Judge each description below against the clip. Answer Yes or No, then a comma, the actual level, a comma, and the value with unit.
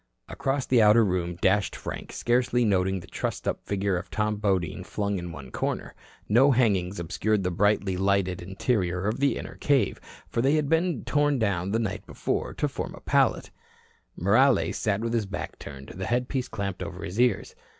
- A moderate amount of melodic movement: Yes, average, 4.6 semitones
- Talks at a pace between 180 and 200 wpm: Yes, average, 185 wpm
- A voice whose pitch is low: Yes, low, 100 Hz